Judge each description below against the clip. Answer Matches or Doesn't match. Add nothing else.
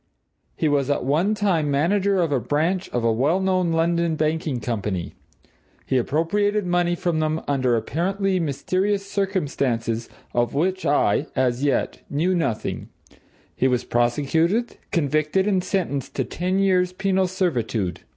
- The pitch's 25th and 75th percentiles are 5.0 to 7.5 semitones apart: Matches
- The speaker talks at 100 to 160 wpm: Matches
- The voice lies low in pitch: Doesn't match